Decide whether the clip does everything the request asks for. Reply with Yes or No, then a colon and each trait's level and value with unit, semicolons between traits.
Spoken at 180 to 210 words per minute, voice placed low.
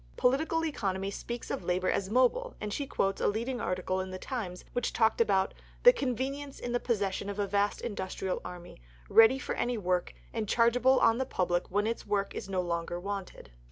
No: average, 200 wpm; high, 205 Hz